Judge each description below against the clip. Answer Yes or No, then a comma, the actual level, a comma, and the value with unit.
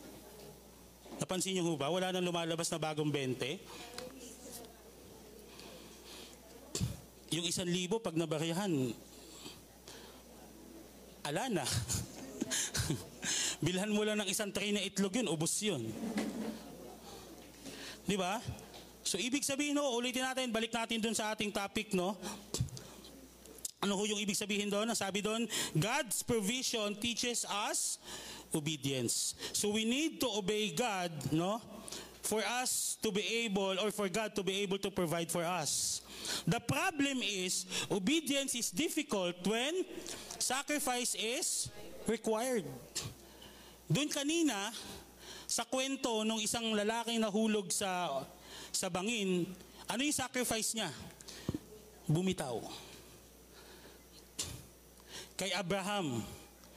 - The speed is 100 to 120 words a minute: Yes, average, 115 wpm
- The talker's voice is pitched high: Yes, high, 210 Hz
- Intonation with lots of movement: No, average, 4.3 semitones